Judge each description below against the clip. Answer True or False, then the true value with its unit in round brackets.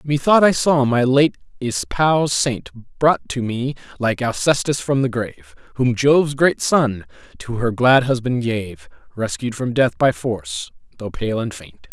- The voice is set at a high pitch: False (130 Hz)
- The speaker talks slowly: False (165 wpm)